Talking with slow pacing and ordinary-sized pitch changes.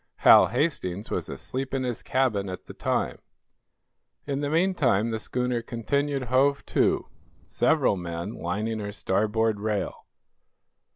Yes: slow, 130 wpm; average, 4.7 semitones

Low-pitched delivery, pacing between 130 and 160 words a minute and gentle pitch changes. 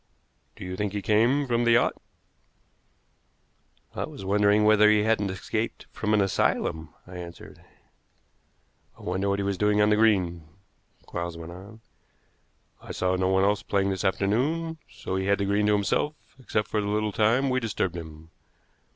No: low, 100 Hz; average, 175 wpm; narrow, 2.3 semitones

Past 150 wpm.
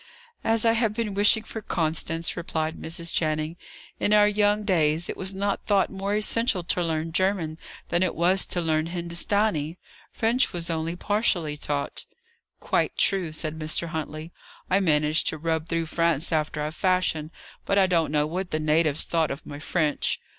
Yes: average, 175 wpm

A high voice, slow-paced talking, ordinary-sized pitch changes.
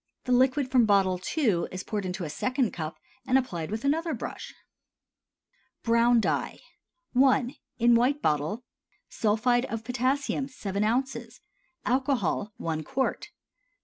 Yes: high, 240 Hz; slow, 130 wpm; average, 4.6 semitones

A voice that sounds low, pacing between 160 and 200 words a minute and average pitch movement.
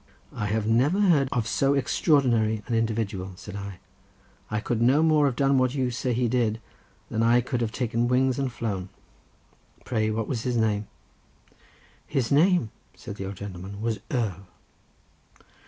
Yes: low, 115 Hz; average, 165 wpm; average, 3.3 semitones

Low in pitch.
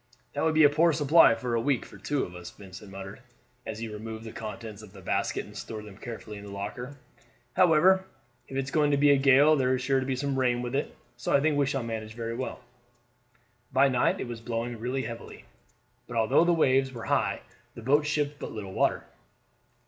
Yes: low, 125 Hz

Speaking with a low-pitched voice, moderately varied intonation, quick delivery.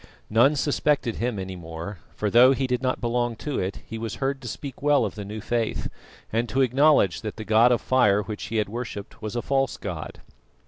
Yes: low, 115 Hz; average, 3.7 semitones; fast, 220 wpm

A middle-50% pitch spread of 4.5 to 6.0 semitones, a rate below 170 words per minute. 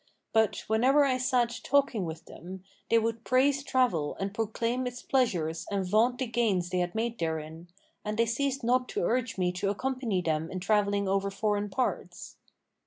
No: average, 5.2 semitones; average, 175 wpm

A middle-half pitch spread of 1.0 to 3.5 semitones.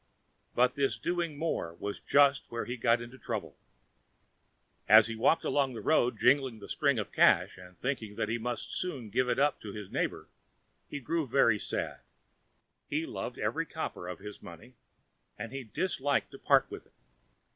No: average, 4.5 semitones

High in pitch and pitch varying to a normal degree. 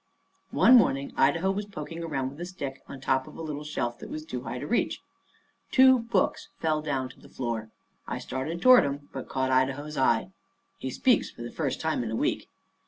No: medium, 145 Hz; average, 4.3 semitones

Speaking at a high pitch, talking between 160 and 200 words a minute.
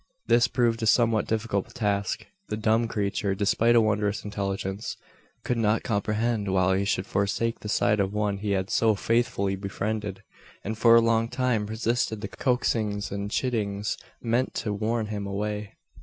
No: low, 105 Hz; average, 165 wpm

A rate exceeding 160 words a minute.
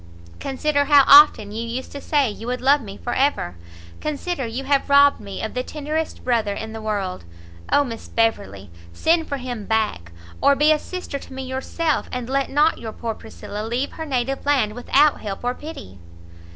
Yes: average, 190 wpm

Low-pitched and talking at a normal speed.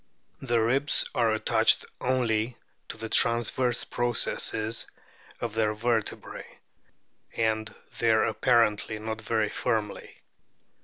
No: low, 115 Hz; slow, 100 wpm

